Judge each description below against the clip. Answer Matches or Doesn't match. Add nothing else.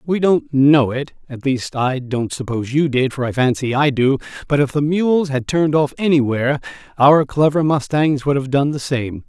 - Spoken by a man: Matches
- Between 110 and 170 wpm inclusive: Doesn't match